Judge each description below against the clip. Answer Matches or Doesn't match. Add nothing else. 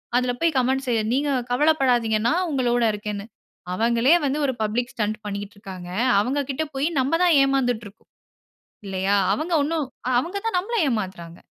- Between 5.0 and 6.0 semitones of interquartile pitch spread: Matches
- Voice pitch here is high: Matches